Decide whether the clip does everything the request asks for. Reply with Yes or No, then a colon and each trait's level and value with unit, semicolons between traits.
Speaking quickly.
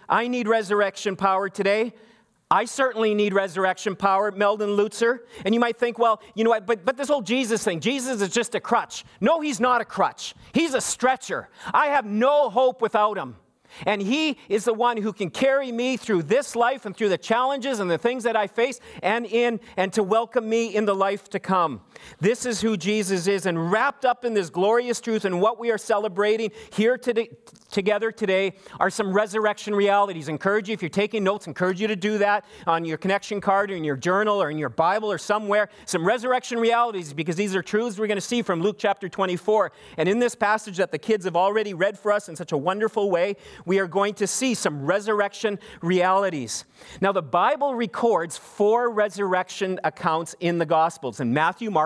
Yes: fast, 210 wpm